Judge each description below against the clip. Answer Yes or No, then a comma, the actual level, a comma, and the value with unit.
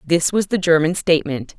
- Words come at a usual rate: Yes, average, 190 wpm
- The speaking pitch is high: No, medium, 165 Hz